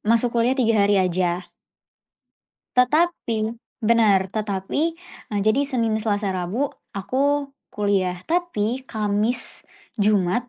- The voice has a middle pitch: No, high, 215 Hz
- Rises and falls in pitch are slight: No, average, 3.8 semitones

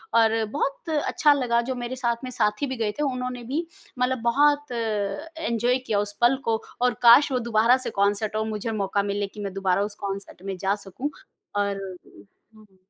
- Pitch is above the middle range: Yes, high, 230 Hz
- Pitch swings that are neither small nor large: Yes, average, 3.9 semitones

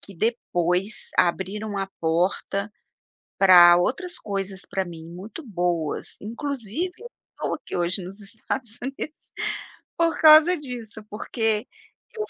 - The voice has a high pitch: Yes, high, 205 Hz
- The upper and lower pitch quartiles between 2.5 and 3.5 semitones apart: No, wide, 5.6 semitones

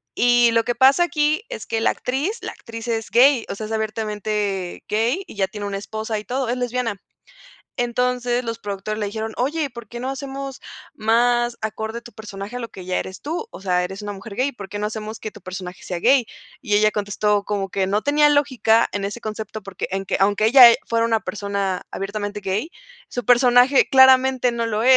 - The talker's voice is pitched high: Yes, high, 225 Hz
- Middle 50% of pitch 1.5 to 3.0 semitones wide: No, average, 3.4 semitones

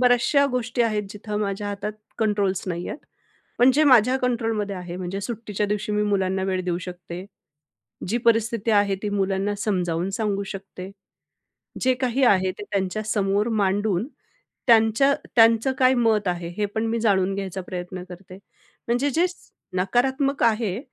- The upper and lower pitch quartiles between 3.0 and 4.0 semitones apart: Yes, average, 3.4 semitones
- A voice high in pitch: Yes, high, 210 Hz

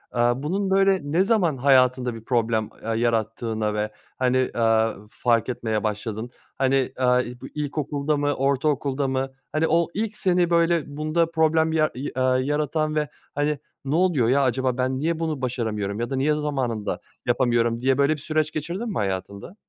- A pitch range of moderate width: Yes, average, 4.5 semitones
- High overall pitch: No, low, 135 Hz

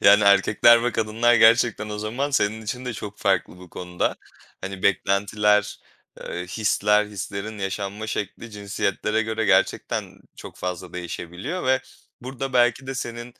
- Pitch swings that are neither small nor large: Yes, average, 3.1 semitones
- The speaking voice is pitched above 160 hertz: No, low, 105 Hz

